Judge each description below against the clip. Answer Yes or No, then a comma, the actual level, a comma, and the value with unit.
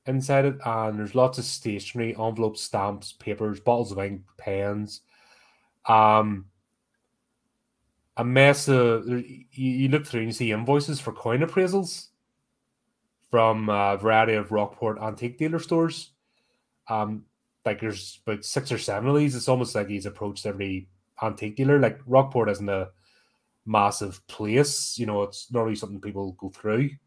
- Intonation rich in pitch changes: No, average, 4.1 semitones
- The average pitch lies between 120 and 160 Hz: No, low, 110 Hz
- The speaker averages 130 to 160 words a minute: Yes, average, 150 wpm